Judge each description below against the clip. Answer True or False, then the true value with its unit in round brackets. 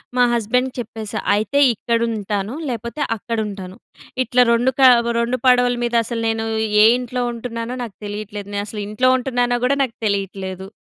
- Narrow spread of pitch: False (3.0 semitones)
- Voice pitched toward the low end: False (230 Hz)